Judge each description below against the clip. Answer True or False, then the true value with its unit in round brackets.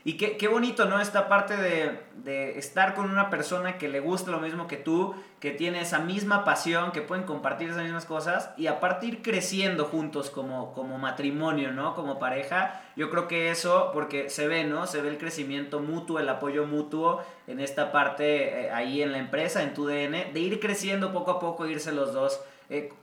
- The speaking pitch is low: False (160 Hz)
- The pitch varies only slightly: False (4.1 semitones)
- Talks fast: True (205 wpm)